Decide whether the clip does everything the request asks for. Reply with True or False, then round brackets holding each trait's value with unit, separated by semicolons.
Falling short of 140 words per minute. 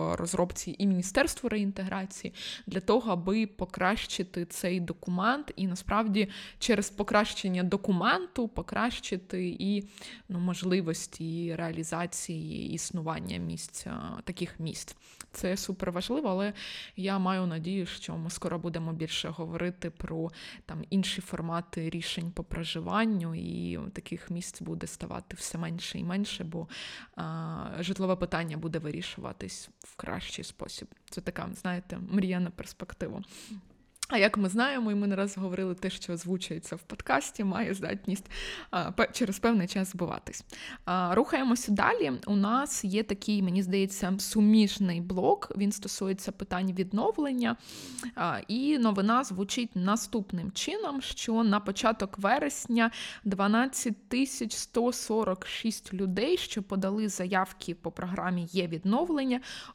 True (125 wpm)